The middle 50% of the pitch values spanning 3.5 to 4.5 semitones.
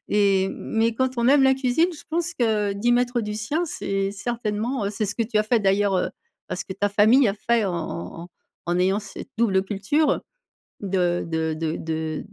Yes: average, 3.9 semitones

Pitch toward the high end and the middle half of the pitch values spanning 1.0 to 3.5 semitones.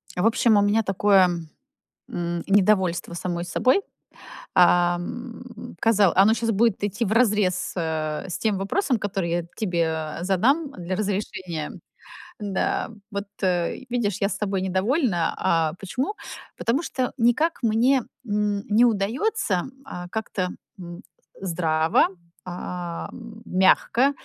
No: high, 200 Hz; average, 4.3 semitones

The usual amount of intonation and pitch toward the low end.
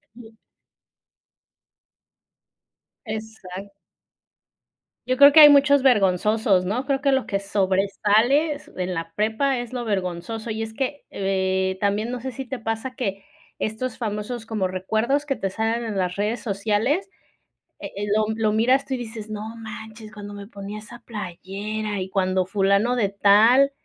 No: average, 3.5 semitones; high, 215 Hz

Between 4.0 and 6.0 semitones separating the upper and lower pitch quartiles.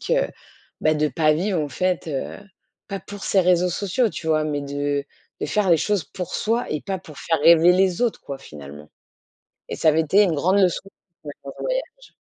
Yes: average, 4.5 semitones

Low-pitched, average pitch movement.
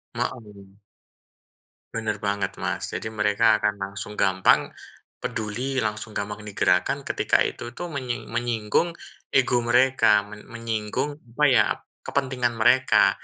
Yes: low, 115 Hz; average, 3.2 semitones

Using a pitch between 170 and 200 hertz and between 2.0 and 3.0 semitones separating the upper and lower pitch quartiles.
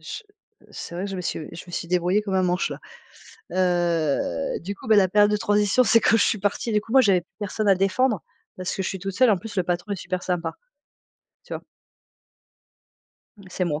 Yes: high, 190 Hz; average, 2.7 semitones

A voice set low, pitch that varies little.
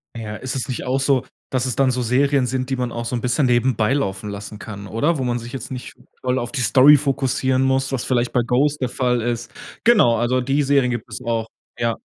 Yes: low, 125 Hz; narrow, 2.0 semitones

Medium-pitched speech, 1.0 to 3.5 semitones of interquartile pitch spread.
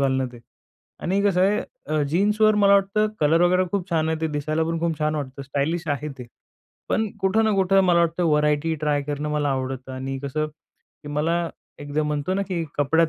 No: medium, 160 Hz; average, 4.0 semitones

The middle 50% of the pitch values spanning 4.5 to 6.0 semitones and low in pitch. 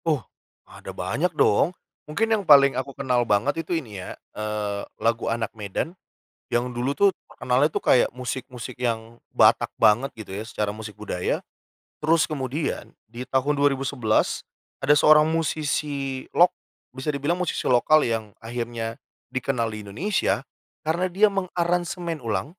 Yes: average, 5.2 semitones; low, 130 Hz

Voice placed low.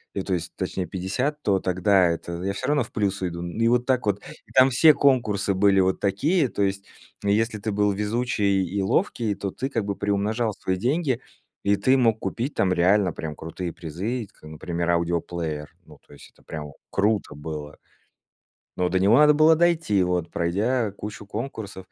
Yes: low, 100 Hz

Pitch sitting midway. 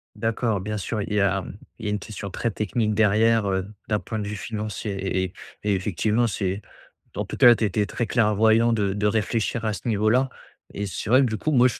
No: low, 105 Hz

